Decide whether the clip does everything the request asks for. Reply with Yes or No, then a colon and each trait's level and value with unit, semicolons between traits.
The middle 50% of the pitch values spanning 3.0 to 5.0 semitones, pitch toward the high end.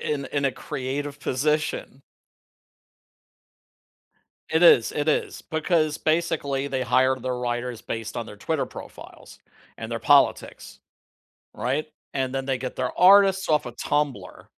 No: average, 3.3 semitones; medium, 140 Hz